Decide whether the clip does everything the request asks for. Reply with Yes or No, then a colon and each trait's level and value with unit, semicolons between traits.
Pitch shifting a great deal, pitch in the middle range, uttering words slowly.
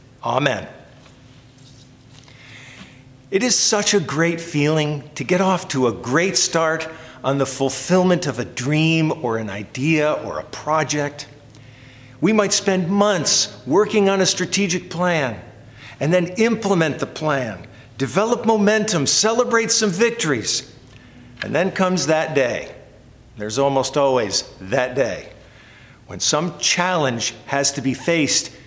Yes: wide, 6.0 semitones; medium, 145 Hz; slow, 130 wpm